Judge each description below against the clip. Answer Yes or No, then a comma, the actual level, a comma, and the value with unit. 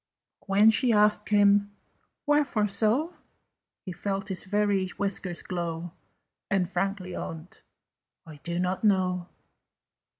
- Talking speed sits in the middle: No, slow, 120 wpm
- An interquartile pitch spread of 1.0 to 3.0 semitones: Yes, narrow, 2.5 semitones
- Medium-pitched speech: No, high, 195 Hz